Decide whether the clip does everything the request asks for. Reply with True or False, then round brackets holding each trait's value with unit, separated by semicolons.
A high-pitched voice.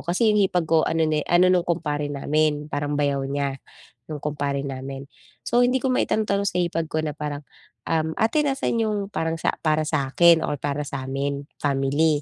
False (155 Hz)